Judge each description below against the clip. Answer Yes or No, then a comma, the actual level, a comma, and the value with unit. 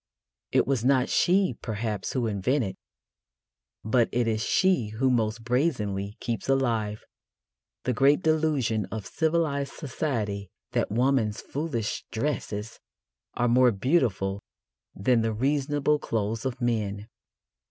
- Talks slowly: Yes, slow, 120 wpm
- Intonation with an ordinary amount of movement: Yes, average, 4.4 semitones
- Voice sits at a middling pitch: No, low, 120 Hz